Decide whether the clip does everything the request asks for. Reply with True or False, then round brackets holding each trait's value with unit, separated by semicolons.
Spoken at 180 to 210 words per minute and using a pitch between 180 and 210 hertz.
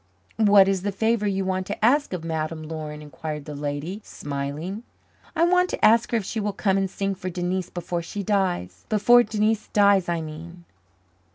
True (190 wpm; 190 Hz)